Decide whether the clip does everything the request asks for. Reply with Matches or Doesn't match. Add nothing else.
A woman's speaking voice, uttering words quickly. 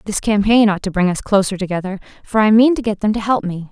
Matches